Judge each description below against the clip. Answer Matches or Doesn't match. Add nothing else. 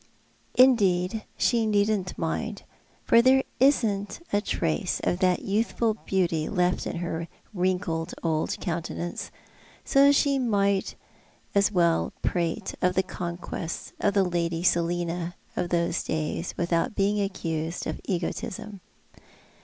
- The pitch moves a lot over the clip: Doesn't match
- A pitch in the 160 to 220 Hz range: Matches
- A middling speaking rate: Doesn't match